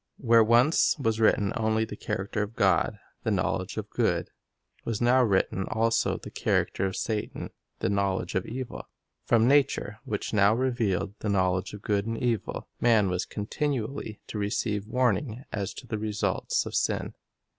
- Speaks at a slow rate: No, average, 165 wpm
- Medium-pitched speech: No, low, 110 Hz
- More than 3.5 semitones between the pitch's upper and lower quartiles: No, average, 2.7 semitones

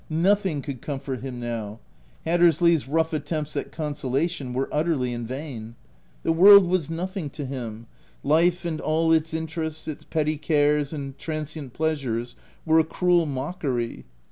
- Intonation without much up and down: No, average, 3.4 semitones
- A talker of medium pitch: Yes, medium, 155 Hz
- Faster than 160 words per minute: No, average, 150 wpm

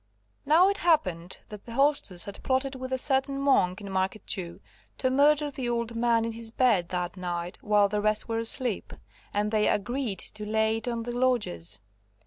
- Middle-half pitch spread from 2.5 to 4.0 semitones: No, average, 4.6 semitones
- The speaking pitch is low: No, high, 225 Hz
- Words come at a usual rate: Yes, average, 190 wpm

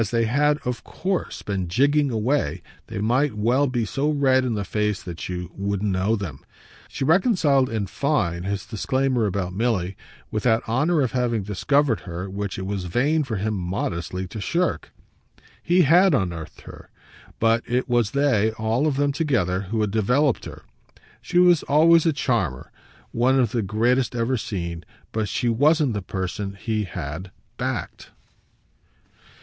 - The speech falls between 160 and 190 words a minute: Yes, average, 165 wpm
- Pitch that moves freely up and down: Yes, wide, 5.9 semitones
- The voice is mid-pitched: No, low, 115 Hz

